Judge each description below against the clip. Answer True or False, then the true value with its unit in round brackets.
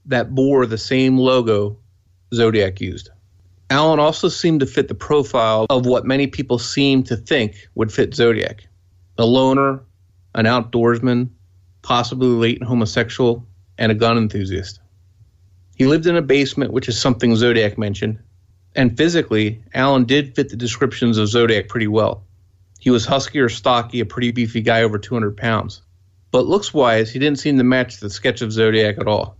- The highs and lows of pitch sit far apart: False (4.0 semitones)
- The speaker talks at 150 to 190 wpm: True (170 wpm)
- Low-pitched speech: True (115 Hz)